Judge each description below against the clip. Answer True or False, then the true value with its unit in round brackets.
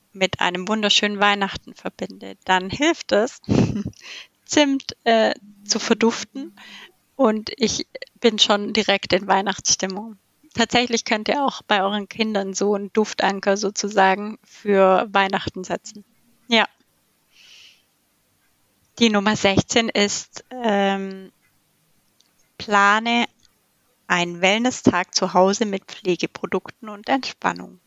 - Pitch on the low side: False (205 Hz)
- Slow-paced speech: True (105 wpm)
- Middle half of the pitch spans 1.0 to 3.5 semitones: True (2.9 semitones)